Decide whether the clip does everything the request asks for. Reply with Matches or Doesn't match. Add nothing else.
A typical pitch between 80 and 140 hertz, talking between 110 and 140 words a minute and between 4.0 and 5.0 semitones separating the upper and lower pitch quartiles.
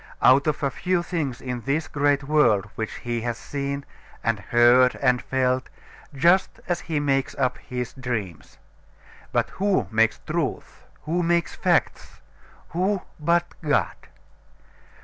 Matches